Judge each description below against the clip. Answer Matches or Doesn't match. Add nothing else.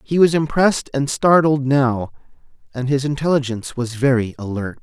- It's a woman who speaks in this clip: Doesn't match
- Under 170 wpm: Matches